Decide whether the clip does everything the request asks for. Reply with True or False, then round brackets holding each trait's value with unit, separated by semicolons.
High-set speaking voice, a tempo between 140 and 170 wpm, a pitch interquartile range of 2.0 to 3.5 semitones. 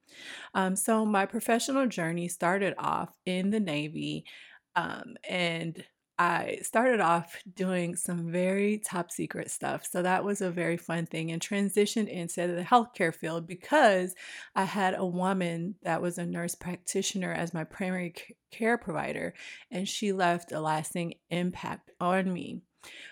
False (180 Hz; 150 wpm; 2.8 semitones)